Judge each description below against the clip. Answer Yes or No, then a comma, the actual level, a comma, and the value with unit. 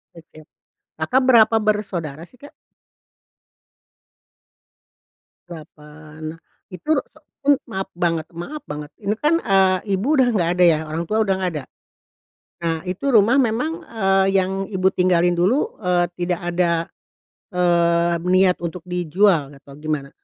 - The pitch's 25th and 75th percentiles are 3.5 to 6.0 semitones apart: Yes, average, 4.1 semitones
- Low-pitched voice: No, medium, 180 Hz